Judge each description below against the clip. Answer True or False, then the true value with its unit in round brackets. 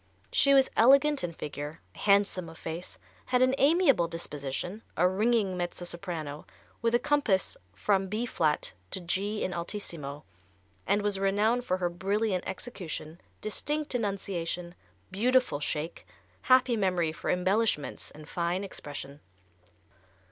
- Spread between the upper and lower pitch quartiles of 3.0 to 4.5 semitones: False (5.0 semitones)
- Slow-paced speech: True (130 wpm)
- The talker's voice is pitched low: False (190 Hz)